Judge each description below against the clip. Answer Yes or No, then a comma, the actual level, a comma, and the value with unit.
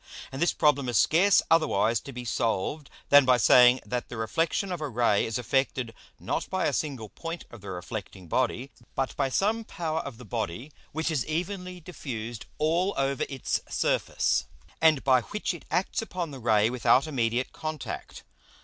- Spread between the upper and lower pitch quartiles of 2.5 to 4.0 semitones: No, average, 5.2 semitones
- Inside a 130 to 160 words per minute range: No, average, 175 wpm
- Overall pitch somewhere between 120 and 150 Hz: Yes, low, 135 Hz